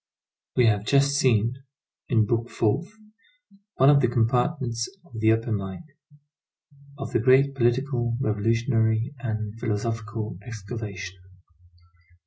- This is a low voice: Yes, low, 115 Hz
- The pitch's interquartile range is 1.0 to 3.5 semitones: Yes, average, 2.8 semitones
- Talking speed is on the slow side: Yes, slow, 115 wpm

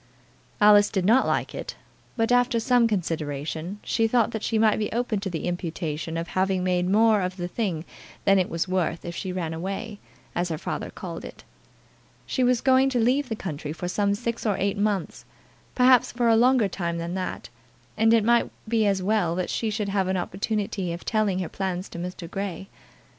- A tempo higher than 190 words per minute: Yes, average, 200 wpm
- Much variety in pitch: No, average, 4.0 semitones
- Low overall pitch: No, high, 195 Hz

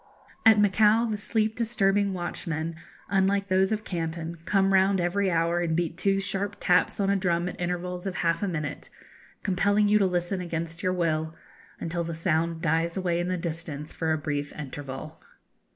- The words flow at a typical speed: Yes, average, 180 wpm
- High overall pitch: No, medium, 180 Hz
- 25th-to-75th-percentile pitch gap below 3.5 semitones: Yes, average, 3.0 semitones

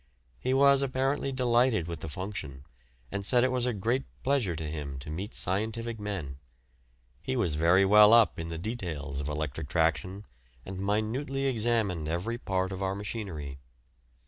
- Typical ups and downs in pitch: No, wide, 6.4 semitones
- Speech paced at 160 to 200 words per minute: Yes, average, 165 wpm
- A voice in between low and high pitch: No, low, 100 Hz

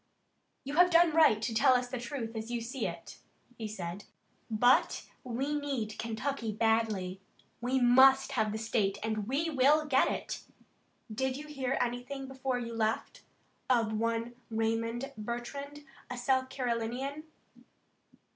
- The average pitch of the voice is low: No, high, 245 Hz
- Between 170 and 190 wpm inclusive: No, average, 145 wpm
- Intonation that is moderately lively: Yes, average, 3.3 semitones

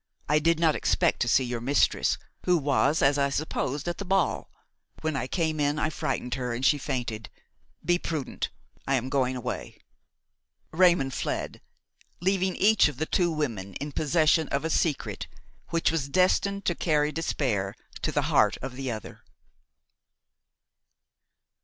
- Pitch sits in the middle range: Yes, medium, 150 Hz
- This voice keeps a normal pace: Yes, average, 160 wpm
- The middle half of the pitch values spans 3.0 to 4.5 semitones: Yes, average, 4.1 semitones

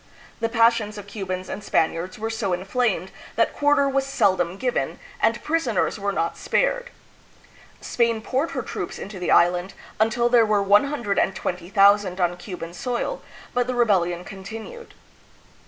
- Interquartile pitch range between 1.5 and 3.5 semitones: No, average, 4.5 semitones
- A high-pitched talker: Yes, high, 210 Hz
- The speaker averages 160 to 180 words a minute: No, average, 145 wpm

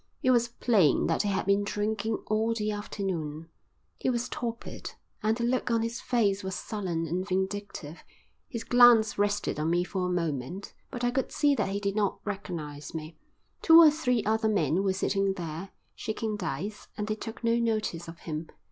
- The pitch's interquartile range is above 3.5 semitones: Yes, average, 4.2 semitones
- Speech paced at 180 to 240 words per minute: Yes, average, 190 wpm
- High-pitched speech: Yes, high, 205 Hz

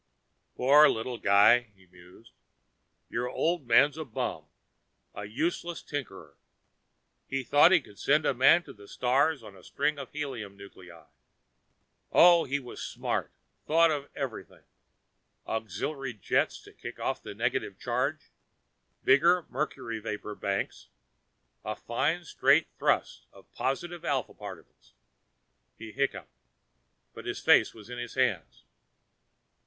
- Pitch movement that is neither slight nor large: No, wide, 5.9 semitones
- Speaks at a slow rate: Yes, slow, 125 wpm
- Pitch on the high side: No, low, 125 Hz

